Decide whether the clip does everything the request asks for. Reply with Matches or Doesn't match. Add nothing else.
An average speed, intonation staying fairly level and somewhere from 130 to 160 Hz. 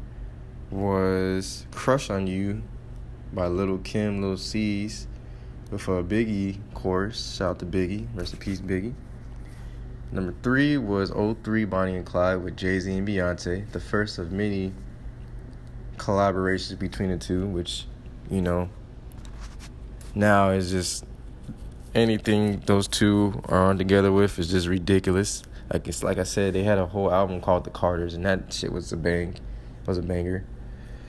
Doesn't match